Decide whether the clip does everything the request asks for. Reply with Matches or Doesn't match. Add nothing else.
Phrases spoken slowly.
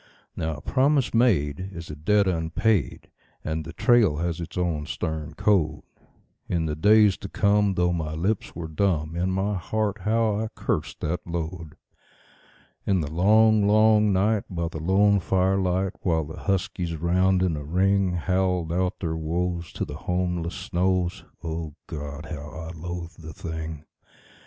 Doesn't match